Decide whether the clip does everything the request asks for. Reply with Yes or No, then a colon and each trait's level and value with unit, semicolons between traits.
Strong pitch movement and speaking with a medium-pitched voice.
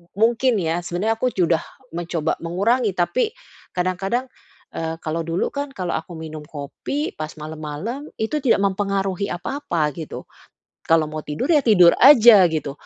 Yes: wide, 6.0 semitones; medium, 180 Hz